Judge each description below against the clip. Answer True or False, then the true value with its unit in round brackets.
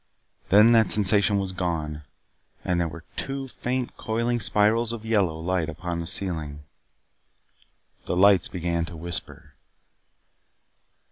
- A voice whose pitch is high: False (95 Hz)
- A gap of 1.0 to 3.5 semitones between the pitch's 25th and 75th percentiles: False (4.7 semitones)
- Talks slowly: True (125 wpm)